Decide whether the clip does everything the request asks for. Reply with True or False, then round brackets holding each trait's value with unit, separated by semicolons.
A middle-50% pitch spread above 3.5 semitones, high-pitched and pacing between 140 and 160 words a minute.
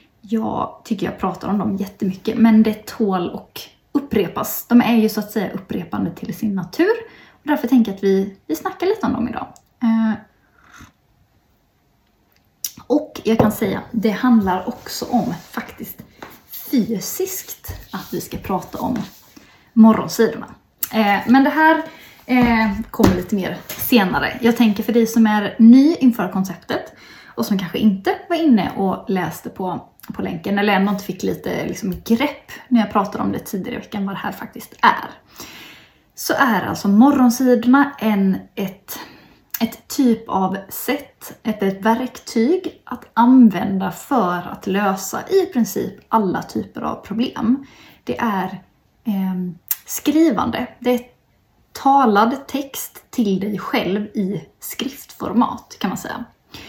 True (4.1 semitones; 225 Hz; 150 wpm)